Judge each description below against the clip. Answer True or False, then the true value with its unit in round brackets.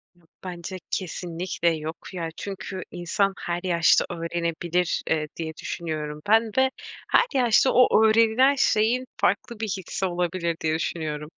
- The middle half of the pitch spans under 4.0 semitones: False (4.5 semitones)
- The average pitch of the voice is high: False (175 Hz)